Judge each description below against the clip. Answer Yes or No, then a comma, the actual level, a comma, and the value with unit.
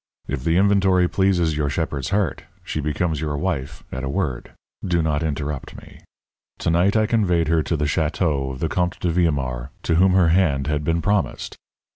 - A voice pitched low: Yes, very low, 80 Hz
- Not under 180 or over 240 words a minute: Yes, average, 190 wpm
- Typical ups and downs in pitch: Yes, average, 3.7 semitones